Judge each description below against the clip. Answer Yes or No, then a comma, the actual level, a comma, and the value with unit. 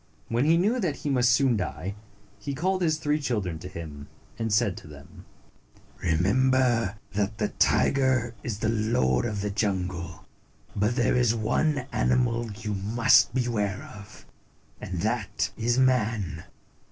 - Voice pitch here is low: Yes, low, 110 Hz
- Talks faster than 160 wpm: No, average, 155 wpm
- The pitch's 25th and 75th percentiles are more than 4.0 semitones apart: Yes, average, 4.5 semitones